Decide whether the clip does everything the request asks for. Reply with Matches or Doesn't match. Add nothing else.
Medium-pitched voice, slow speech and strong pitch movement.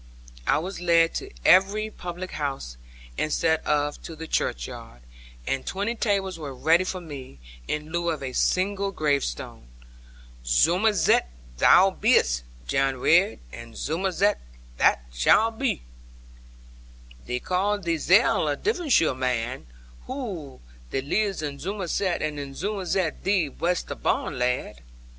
Matches